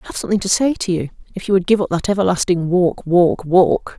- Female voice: Yes, female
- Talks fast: Yes, fast, 255 wpm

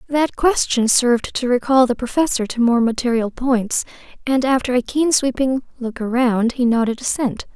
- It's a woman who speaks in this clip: Yes, female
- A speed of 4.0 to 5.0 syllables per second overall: Yes, 4.9 syllables/s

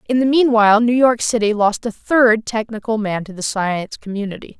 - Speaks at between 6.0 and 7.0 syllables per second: No, 5.4 syllables/s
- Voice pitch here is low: No, high, 225 Hz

